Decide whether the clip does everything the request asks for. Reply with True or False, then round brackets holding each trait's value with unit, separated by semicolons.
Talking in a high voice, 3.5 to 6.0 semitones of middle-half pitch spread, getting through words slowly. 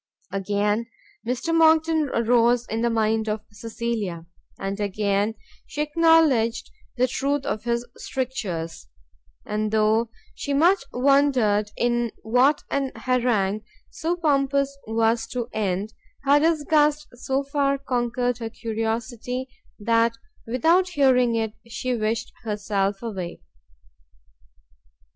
True (235 Hz; 4.3 semitones; 110 wpm)